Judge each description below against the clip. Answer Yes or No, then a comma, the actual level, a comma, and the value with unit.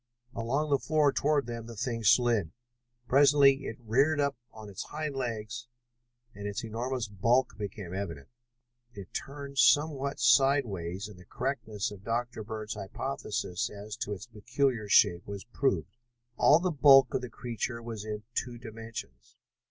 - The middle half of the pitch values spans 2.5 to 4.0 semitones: No, average, 4.5 semitones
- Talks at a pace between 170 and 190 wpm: No, average, 155 wpm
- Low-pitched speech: Yes, low, 115 Hz